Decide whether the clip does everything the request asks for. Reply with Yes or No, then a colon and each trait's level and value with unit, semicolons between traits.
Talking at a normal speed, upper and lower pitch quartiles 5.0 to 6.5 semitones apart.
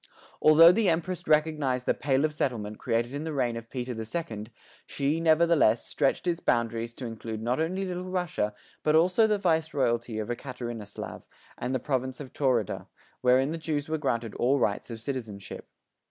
Yes: average, 180 wpm; wide, 5.5 semitones